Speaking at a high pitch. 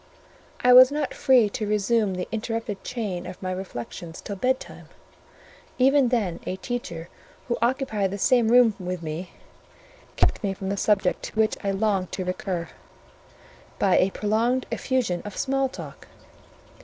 Yes: high, 210 Hz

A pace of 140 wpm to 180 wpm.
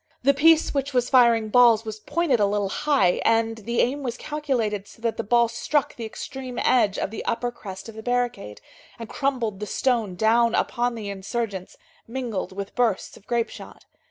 No: average, 190 wpm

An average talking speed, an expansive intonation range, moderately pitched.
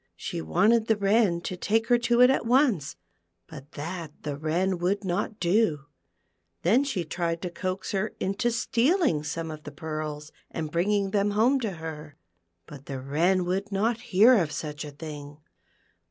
Yes: average, 170 wpm; wide, 5.9 semitones; medium, 180 Hz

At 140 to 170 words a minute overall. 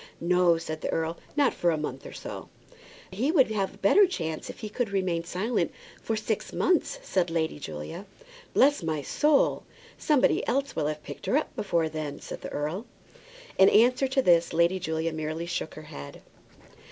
No: average, 185 wpm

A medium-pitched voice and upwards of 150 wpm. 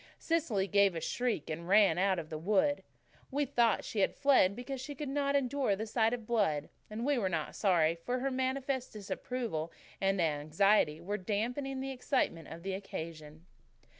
No: high, 210 Hz; average, 180 wpm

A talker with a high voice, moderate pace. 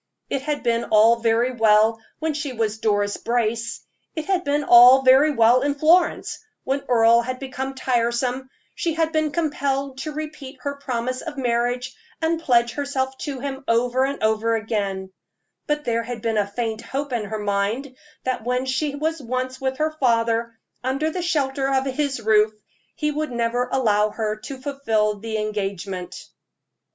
Yes: very high, 255 Hz; average, 170 wpm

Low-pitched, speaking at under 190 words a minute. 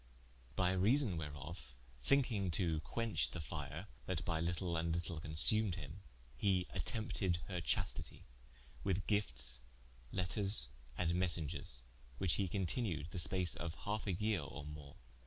Yes: very low, 90 Hz; average, 140 wpm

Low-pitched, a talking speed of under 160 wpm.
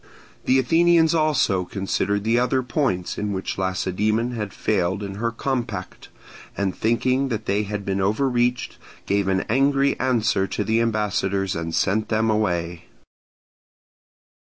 Yes: low, 110 Hz; slow, 135 wpm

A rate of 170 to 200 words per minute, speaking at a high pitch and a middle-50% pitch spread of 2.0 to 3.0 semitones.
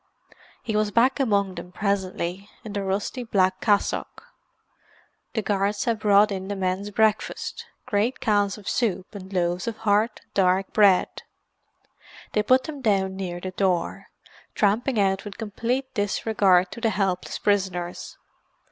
No: average, 140 wpm; high, 200 Hz; narrow, 2.4 semitones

